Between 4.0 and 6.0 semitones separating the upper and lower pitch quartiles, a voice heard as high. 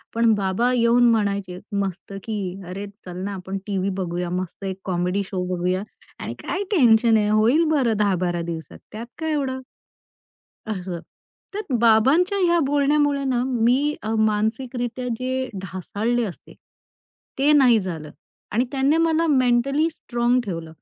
Yes: wide, 5.6 semitones; high, 225 Hz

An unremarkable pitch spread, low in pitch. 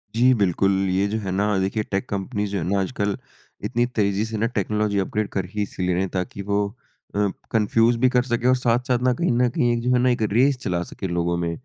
Yes: average, 3.8 semitones; low, 105 Hz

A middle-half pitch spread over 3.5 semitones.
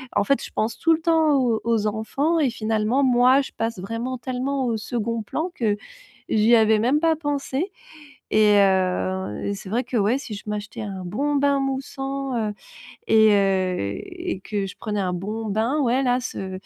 Yes: average, 4.6 semitones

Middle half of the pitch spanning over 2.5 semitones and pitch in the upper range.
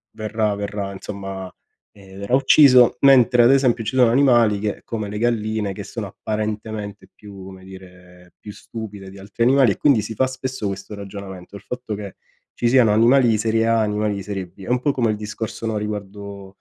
No: average, 2.9 semitones; low, 105 Hz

